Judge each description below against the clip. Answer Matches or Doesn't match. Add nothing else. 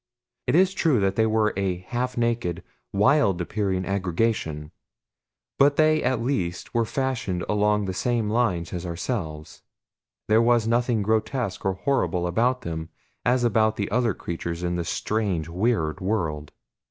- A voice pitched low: Matches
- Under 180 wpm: Matches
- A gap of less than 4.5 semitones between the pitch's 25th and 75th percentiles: Doesn't match